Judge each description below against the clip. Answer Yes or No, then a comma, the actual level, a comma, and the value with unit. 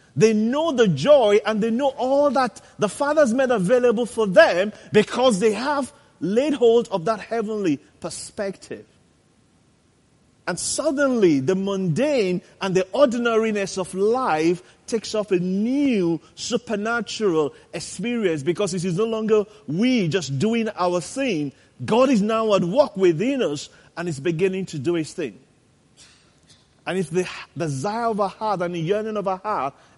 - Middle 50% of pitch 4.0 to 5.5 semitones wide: Yes, average, 4.5 semitones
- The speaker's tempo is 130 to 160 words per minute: Yes, average, 150 wpm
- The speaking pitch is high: Yes, high, 210 Hz